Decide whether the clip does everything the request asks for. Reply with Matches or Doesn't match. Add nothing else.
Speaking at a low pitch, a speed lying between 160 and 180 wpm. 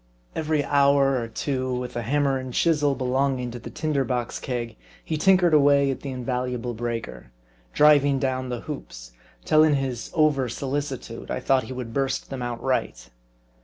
Matches